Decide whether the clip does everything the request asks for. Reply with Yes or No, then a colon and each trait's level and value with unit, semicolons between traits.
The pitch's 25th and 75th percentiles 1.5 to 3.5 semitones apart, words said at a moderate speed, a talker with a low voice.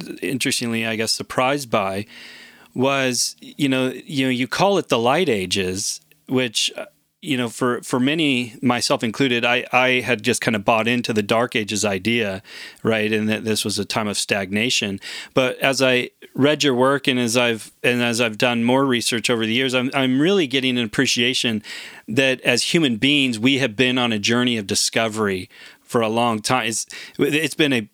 Yes: average, 2.7 semitones; average, 190 wpm; low, 125 Hz